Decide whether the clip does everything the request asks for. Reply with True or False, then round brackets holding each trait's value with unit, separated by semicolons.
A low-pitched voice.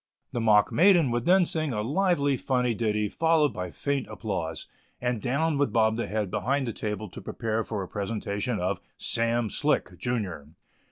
True (115 Hz)